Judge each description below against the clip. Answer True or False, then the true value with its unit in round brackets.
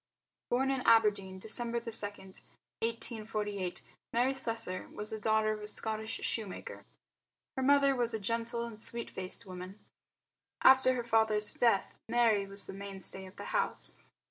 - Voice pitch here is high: True (220 Hz)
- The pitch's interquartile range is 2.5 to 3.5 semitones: True (2.8 semitones)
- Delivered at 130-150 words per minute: True (145 wpm)